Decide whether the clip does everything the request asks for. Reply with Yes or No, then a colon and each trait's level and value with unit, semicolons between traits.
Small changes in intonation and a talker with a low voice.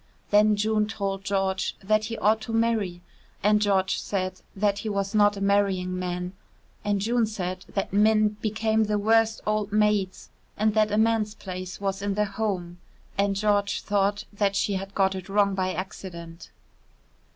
No: narrow, 1.8 semitones; high, 205 Hz